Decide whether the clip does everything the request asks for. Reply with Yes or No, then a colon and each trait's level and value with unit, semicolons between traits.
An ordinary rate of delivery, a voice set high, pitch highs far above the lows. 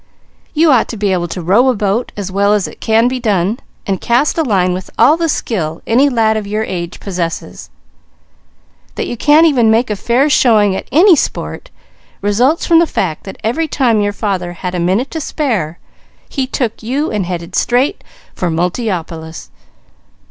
Yes: average, 185 wpm; high, 215 Hz; wide, 5.7 semitones